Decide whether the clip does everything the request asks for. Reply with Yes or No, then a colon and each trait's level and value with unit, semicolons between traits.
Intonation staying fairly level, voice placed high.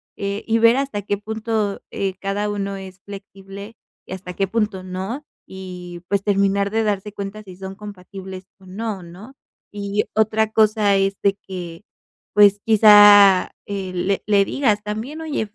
Yes: narrow, 1.8 semitones; high, 200 Hz